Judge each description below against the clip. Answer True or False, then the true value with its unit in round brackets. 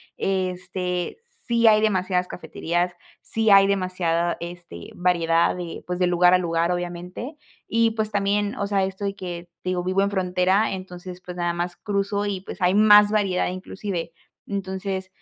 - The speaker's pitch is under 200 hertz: True (185 Hz)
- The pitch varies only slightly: True (2.1 semitones)